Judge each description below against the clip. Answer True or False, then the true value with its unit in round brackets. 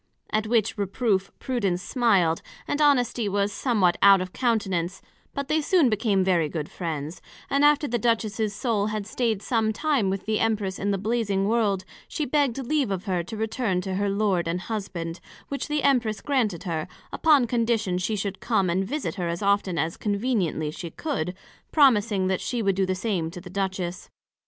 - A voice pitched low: False (205 Hz)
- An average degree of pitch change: True (4.1 semitones)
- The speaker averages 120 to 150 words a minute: False (185 wpm)